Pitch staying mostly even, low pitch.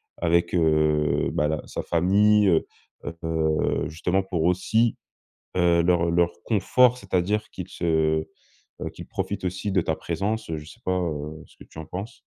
No: average, 3.3 semitones; very low, 85 Hz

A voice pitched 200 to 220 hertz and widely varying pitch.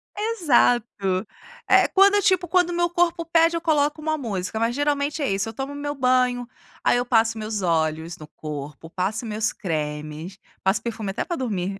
No: high, 240 Hz; wide, 8.1 semitones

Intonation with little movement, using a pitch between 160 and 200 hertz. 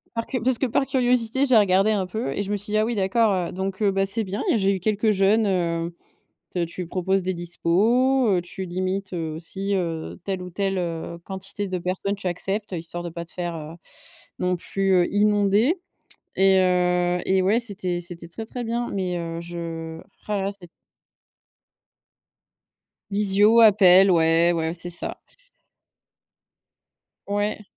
No: average, 3.0 semitones; high, 190 Hz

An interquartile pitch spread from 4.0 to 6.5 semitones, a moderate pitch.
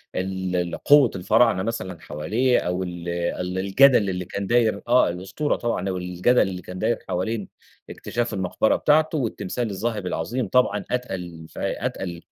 No: average, 4.7 semitones; very low, 95 Hz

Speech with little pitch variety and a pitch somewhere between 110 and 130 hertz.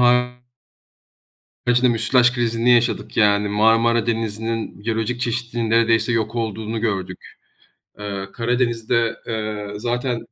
Yes: narrow, 1.7 semitones; low, 115 Hz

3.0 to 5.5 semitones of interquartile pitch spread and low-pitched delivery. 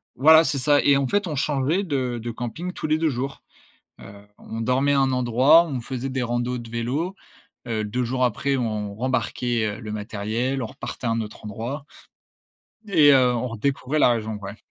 Yes: average, 3.5 semitones; low, 125 Hz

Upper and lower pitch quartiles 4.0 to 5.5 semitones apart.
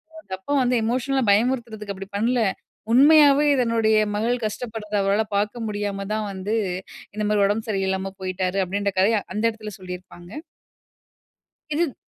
No: average, 3.4 semitones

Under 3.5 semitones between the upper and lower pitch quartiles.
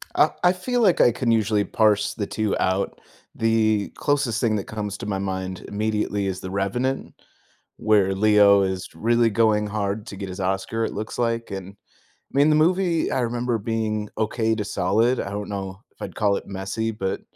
Yes: average, 2.8 semitones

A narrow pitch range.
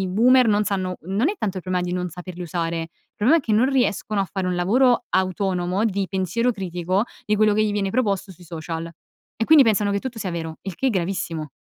No: average, 3.2 semitones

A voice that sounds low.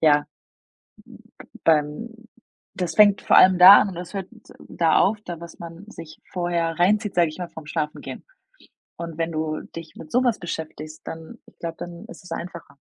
No: medium, 170 Hz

